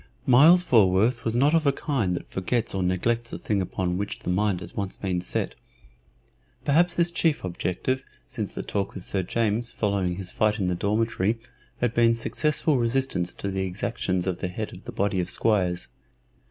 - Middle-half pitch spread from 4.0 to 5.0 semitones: Yes, average, 4.6 semitones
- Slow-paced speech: No, average, 190 wpm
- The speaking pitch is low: Yes, low, 105 Hz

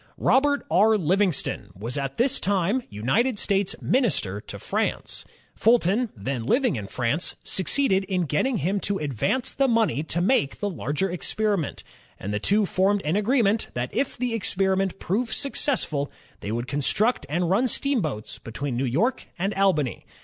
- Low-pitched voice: No, high, 190 Hz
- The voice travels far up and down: Yes, wide, 8.0 semitones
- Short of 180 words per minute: Yes, average, 160 wpm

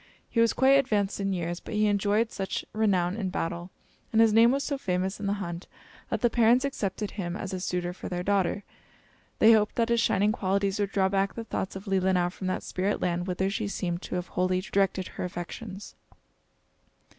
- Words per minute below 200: No, fast, 205 wpm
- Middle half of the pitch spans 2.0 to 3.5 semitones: Yes, average, 2.8 semitones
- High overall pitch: Yes, high, 195 Hz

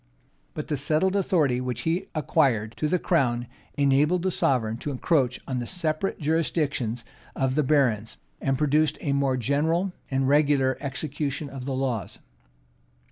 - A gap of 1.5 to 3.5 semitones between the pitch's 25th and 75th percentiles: Yes, average, 3.2 semitones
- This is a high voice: No, medium, 140 Hz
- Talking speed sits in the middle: Yes, average, 150 wpm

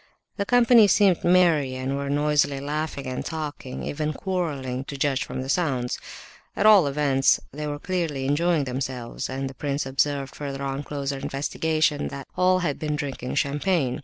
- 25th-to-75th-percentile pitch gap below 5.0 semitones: Yes, average, 2.9 semitones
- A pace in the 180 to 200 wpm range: No, average, 160 wpm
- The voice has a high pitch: No, medium, 145 Hz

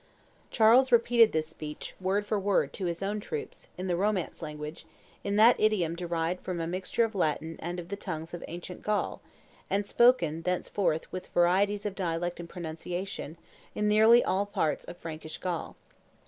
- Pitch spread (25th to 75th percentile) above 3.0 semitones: Yes, average, 3.8 semitones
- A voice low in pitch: No, medium, 185 Hz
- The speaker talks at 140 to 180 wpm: Yes, average, 175 wpm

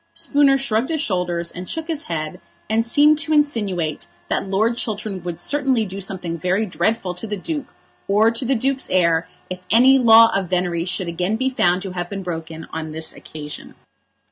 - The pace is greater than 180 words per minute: Yes, average, 190 wpm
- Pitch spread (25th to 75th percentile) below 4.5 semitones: No, wide, 5.5 semitones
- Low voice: No, high, 195 Hz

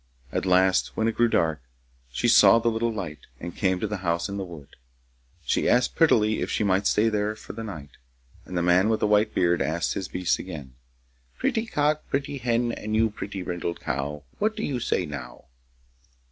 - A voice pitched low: Yes, low, 100 Hz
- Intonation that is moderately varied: Yes, average, 4.5 semitones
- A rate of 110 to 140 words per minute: No, average, 200 wpm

